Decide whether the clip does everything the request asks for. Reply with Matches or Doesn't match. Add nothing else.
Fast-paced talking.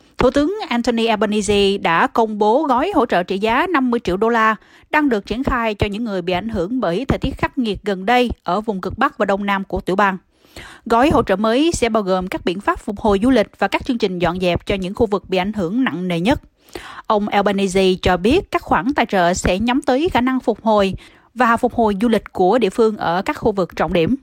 Matches